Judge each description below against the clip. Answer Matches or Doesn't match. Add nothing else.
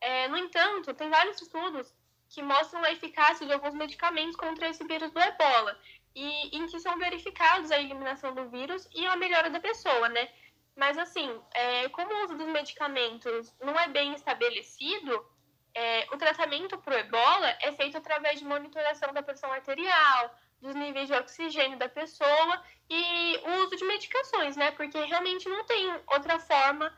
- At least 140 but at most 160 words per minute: Doesn't match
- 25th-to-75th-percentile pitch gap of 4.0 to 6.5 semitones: Doesn't match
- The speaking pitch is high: Matches